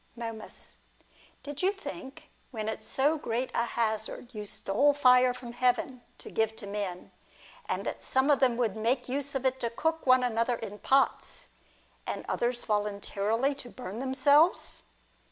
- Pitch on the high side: Yes, high, 245 Hz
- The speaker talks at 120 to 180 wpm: Yes, average, 155 wpm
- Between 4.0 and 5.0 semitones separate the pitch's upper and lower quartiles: No, average, 3.5 semitones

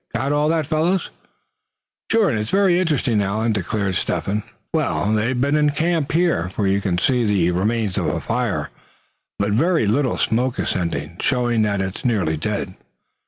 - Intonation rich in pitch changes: Yes, wide, 6.8 semitones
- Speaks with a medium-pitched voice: No, low, 115 Hz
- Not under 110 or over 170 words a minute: No, average, 180 wpm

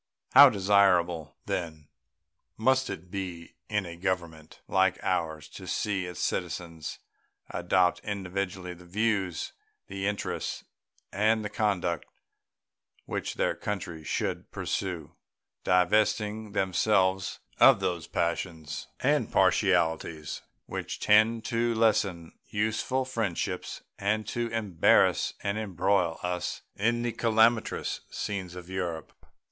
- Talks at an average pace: No, slow, 110 wpm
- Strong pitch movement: No, average, 3.7 semitones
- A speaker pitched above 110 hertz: No, very low, 95 Hz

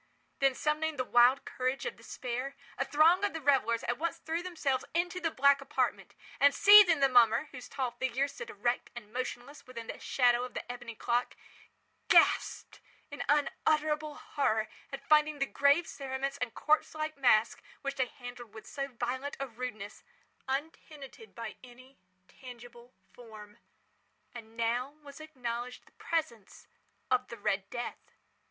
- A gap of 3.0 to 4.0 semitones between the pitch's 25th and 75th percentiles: Yes, average, 3.6 semitones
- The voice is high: Yes, very high, 265 Hz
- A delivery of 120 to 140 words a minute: No, average, 155 wpm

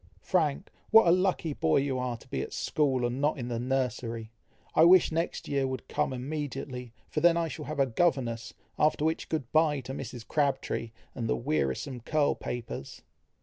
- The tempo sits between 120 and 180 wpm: No, average, 190 wpm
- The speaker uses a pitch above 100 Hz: Yes, low, 135 Hz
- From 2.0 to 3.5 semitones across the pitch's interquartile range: No, average, 4.2 semitones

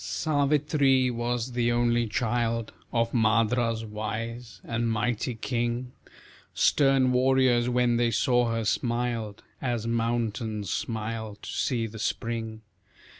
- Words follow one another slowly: Yes, slow, 115 wpm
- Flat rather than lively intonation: Yes, narrow, 1.5 semitones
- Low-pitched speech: Yes, low, 120 Hz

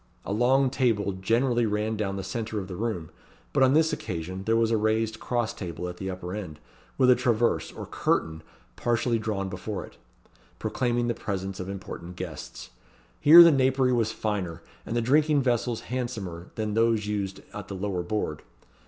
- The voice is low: Yes, low, 110 Hz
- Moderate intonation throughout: Yes, average, 4.1 semitones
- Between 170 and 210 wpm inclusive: Yes, average, 180 wpm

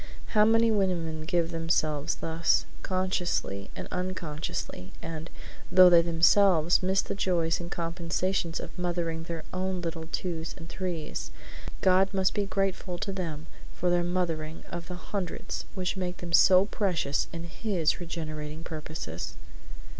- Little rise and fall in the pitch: Yes, narrow, 2.2 semitones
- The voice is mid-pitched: Yes, medium, 175 Hz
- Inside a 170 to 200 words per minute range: No, average, 140 wpm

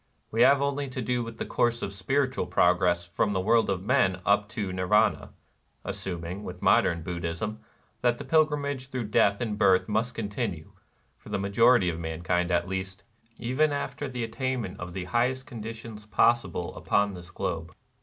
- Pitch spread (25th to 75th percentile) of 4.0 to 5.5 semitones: Yes, average, 4.9 semitones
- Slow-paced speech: No, average, 175 wpm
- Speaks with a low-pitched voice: Yes, low, 105 Hz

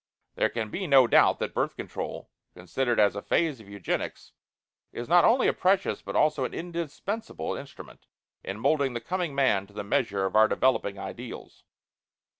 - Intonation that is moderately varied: No, wide, 8.2 semitones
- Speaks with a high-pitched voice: No, low, 125 Hz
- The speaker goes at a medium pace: Yes, average, 175 wpm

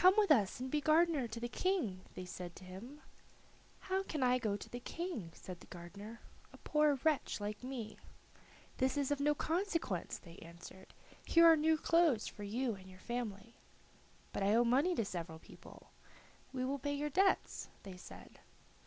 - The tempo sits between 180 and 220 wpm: Yes, average, 185 wpm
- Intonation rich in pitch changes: Yes, wide, 7.3 semitones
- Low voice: No, high, 245 Hz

